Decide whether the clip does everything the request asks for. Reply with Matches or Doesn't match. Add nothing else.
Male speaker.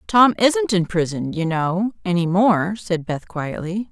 Doesn't match